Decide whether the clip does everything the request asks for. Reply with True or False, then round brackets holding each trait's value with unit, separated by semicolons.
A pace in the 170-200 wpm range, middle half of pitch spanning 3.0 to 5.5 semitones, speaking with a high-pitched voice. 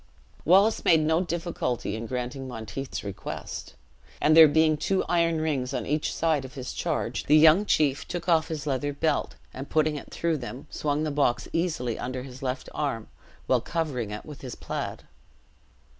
False (175 wpm; 3.9 semitones; 145 Hz)